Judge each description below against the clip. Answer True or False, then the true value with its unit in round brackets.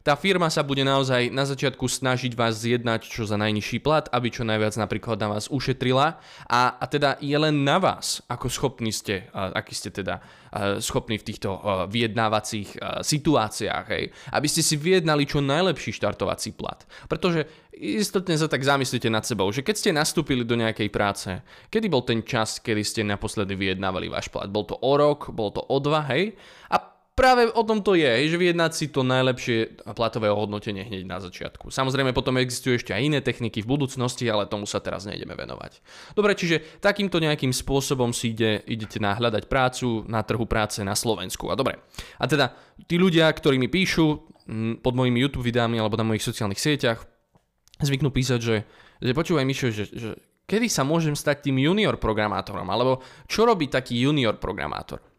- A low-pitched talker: True (125 Hz)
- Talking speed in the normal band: False (180 wpm)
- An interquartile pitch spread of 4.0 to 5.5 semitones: True (5.1 semitones)